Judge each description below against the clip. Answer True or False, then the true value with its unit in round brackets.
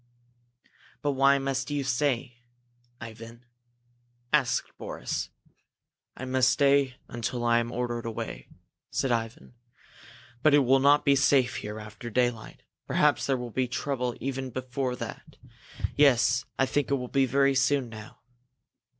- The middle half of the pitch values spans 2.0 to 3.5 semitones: True (2.5 semitones)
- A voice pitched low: True (130 Hz)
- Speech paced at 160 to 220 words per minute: False (140 wpm)